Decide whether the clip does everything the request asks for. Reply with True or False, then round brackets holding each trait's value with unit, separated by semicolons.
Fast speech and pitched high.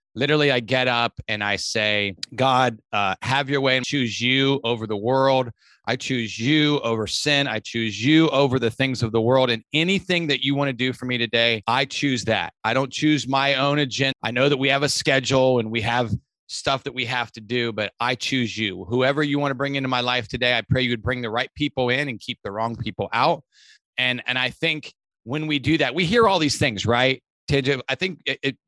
False (235 wpm; 130 Hz)